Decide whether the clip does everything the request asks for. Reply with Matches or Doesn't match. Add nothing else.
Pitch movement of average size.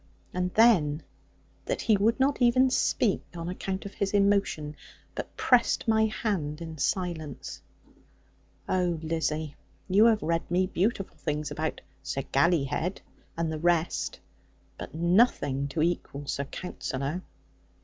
Matches